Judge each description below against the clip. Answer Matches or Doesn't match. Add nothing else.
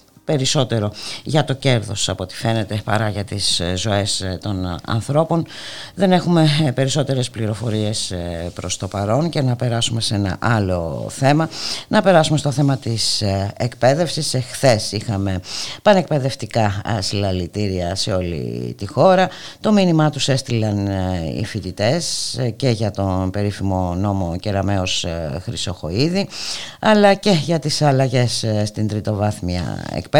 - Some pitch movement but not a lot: Doesn't match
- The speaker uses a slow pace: Doesn't match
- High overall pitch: Doesn't match